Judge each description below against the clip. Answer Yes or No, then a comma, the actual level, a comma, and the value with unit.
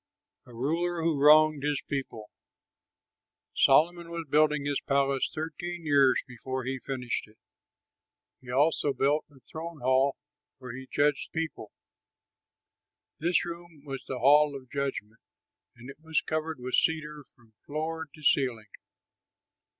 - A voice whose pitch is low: No, medium, 145 Hz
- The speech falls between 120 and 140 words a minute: Yes, slow, 135 wpm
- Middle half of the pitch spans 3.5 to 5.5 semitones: No, average, 3.1 semitones